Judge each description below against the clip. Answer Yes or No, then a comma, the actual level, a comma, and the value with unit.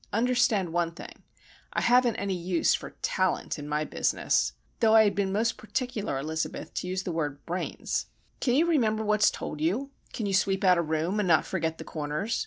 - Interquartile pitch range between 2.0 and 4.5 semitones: No, average, 5.0 semitones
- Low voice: No, high, 190 Hz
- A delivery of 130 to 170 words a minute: No, average, 195 wpm